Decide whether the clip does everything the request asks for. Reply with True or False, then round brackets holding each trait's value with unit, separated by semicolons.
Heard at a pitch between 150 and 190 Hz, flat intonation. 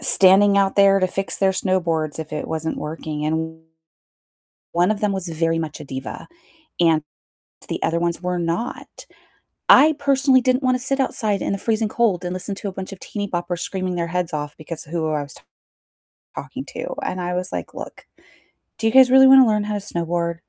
False (185 Hz; 4.1 semitones)